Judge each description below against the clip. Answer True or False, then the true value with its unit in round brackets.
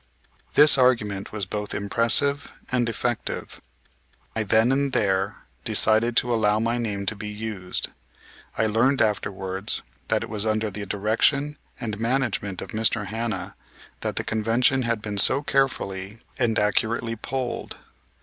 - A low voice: True (110 Hz)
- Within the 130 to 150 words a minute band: True (140 wpm)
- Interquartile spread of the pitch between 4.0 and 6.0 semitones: False (2.7 semitones)